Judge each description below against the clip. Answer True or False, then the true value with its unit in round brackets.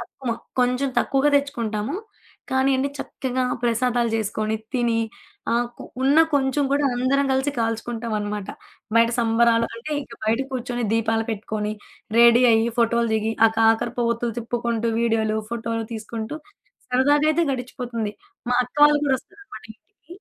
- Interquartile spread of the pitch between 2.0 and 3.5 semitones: True (2.7 semitones)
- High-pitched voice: True (235 Hz)